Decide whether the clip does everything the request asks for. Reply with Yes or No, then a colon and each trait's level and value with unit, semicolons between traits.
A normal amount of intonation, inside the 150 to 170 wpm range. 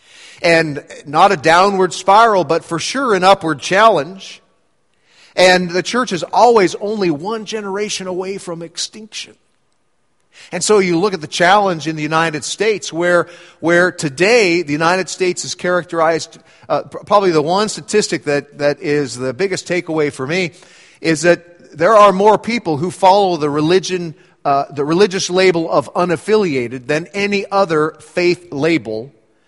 Yes: average, 3.5 semitones; average, 155 wpm